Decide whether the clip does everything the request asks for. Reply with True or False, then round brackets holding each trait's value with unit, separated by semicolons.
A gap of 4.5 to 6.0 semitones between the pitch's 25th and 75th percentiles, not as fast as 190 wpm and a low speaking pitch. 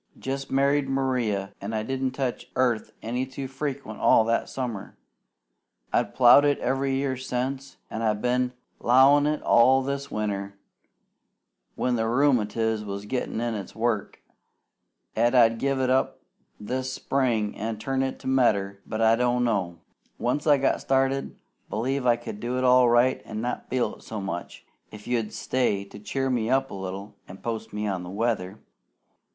False (3.7 semitones; 170 wpm; 120 Hz)